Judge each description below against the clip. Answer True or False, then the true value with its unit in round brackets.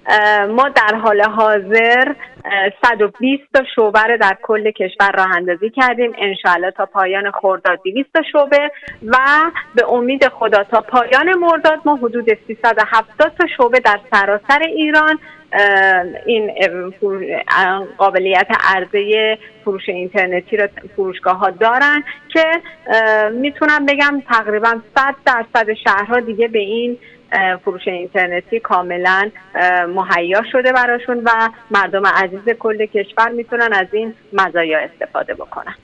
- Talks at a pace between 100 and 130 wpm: True (120 wpm)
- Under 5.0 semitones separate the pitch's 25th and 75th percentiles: True (4.2 semitones)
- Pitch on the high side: True (220 Hz)